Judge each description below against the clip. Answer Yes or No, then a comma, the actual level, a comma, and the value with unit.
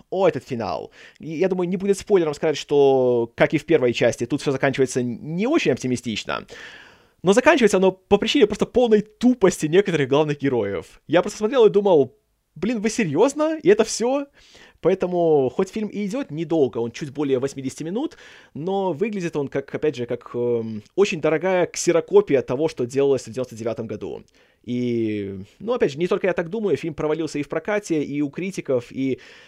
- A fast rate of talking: Yes, fast, 180 wpm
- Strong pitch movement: Yes, wide, 7.1 semitones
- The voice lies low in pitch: No, medium, 160 Hz